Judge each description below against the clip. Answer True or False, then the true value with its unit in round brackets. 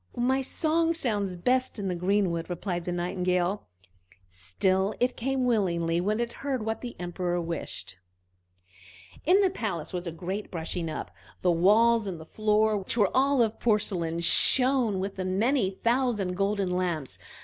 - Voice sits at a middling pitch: False (195 Hz)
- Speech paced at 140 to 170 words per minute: True (155 wpm)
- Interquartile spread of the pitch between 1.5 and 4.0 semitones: False (5.0 semitones)